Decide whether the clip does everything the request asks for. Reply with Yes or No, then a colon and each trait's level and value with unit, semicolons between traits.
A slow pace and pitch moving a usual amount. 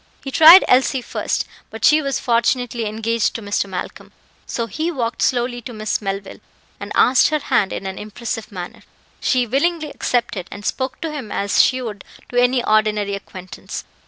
No: average, 175 wpm; average, 3.8 semitones